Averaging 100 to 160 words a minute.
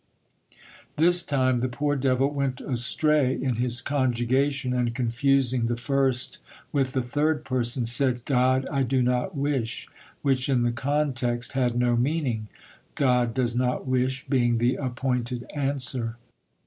Yes: average, 140 wpm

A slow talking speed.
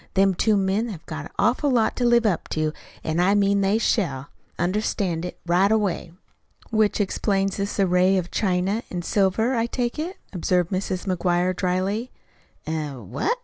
No: average, 170 wpm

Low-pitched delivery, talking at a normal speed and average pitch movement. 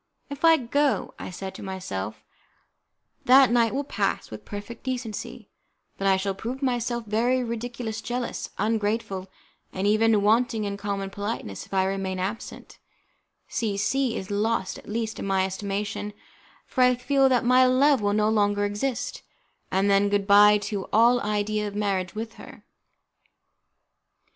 No: high, 210 Hz; average, 160 wpm; average, 3.2 semitones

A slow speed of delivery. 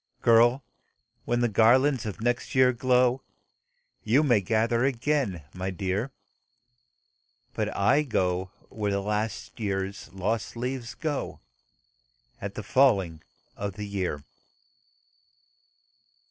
Yes: slow, 110 wpm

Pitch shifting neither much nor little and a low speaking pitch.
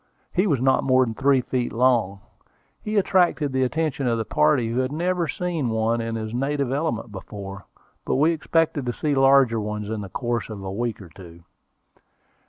Yes: average, 4.6 semitones; low, 125 Hz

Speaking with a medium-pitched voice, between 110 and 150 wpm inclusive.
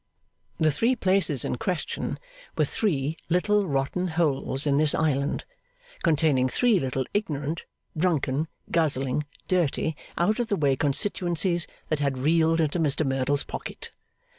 Yes: medium, 155 Hz; slow, 135 wpm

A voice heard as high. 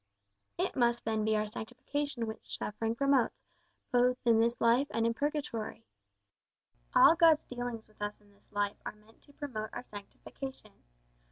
Yes: high, 230 Hz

